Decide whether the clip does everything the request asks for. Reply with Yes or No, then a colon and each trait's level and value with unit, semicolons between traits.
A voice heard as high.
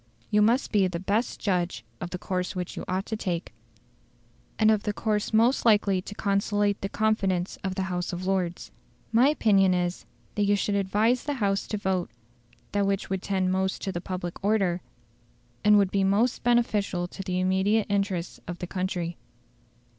Yes: high, 195 Hz